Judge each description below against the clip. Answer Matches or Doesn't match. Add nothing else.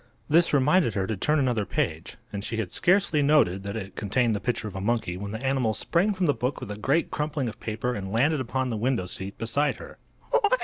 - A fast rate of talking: Matches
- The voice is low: Matches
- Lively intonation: Matches